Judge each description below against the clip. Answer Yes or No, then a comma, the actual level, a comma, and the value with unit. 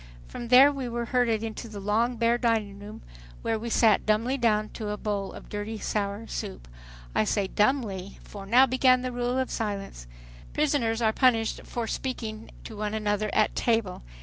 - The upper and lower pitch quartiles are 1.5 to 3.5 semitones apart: Yes, average, 2.7 semitones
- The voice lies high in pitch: Yes, high, 225 Hz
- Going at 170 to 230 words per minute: Yes, average, 175 wpm